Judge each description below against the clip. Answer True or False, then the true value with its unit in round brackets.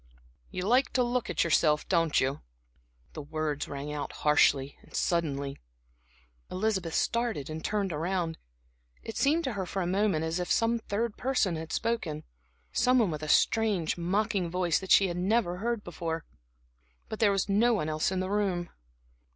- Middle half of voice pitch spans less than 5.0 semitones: False (5.4 semitones)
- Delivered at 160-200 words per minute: True (170 wpm)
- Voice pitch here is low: False (185 Hz)